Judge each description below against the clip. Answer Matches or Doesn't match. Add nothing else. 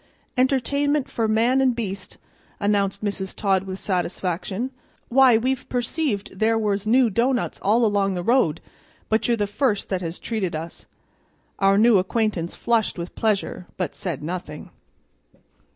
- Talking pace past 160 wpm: Doesn't match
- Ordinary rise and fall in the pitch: Matches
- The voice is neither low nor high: Doesn't match